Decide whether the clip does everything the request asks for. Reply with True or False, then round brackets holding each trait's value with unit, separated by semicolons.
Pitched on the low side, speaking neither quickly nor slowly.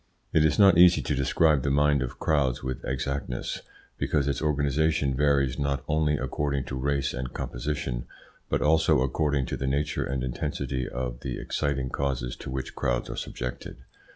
True (70 Hz; 170 wpm)